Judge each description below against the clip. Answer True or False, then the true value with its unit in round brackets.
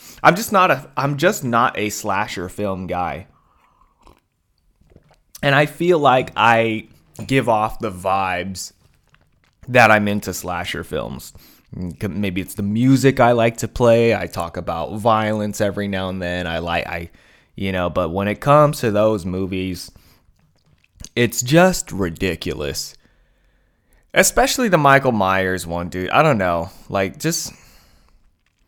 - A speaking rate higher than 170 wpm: False (140 wpm)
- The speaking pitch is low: True (105 Hz)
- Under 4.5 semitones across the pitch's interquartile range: False (5.1 semitones)